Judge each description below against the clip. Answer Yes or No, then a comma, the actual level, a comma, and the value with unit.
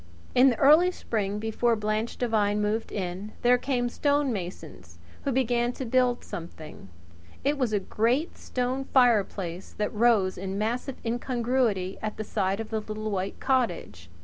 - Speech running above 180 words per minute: No, average, 150 wpm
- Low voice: No, high, 225 Hz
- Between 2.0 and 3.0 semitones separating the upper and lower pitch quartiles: No, average, 3.6 semitones